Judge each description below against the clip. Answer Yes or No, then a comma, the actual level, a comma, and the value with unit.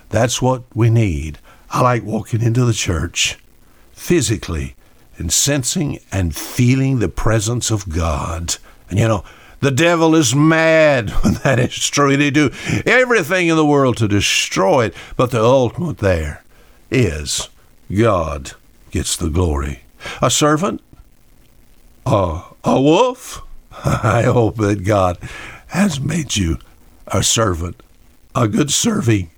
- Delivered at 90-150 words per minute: Yes, slow, 135 wpm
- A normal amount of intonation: No, wide, 7.7 semitones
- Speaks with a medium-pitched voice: No, low, 115 Hz